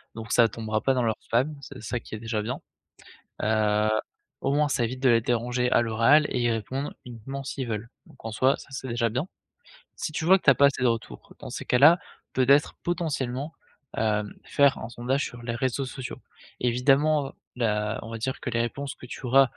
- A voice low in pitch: Yes, low, 125 Hz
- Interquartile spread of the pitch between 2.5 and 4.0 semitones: Yes, average, 3.2 semitones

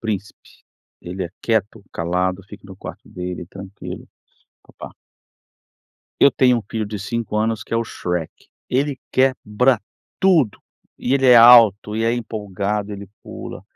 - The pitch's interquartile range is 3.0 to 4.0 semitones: Yes, average, 3.5 semitones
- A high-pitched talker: No, low, 105 Hz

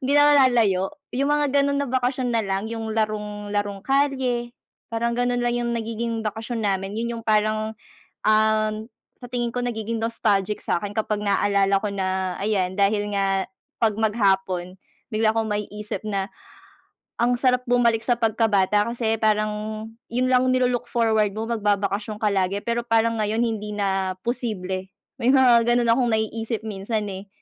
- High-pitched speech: Yes, high, 220 Hz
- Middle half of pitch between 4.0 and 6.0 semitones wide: No, narrow, 2.6 semitones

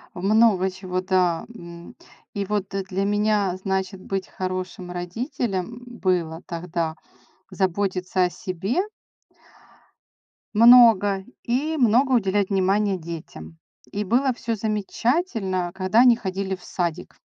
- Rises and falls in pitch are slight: No, average, 3.0 semitones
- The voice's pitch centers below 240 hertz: Yes, high, 190 Hz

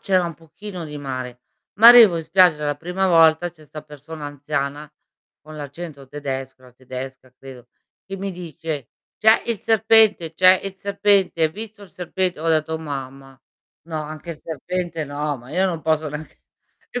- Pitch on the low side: No, medium, 160 Hz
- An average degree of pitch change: Yes, average, 4.1 semitones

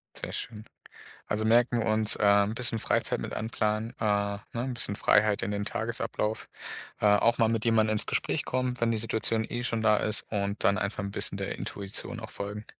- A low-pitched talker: Yes, low, 110 Hz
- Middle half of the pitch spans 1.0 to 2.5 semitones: Yes, narrow, 1.8 semitones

